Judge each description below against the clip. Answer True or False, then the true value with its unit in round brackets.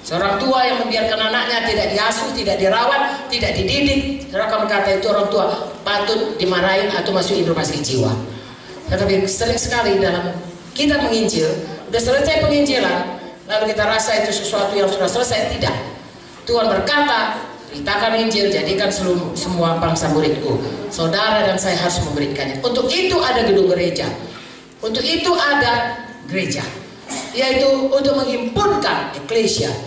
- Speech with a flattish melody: False (5.2 semitones)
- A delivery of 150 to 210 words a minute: False (135 wpm)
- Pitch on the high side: True (210 Hz)